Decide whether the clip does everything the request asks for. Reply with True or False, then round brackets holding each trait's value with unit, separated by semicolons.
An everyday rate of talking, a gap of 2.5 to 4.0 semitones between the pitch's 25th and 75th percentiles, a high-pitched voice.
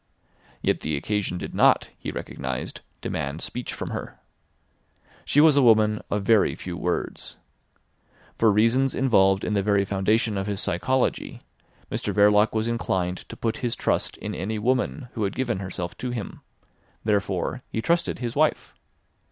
False (160 wpm; 3.4 semitones; 105 Hz)